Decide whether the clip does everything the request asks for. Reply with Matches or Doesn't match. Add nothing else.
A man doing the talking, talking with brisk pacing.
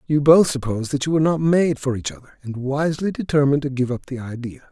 Matches